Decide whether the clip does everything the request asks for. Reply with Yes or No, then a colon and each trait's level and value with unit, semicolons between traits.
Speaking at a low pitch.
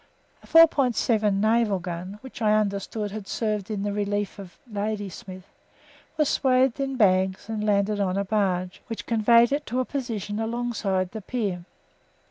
No: high, 210 Hz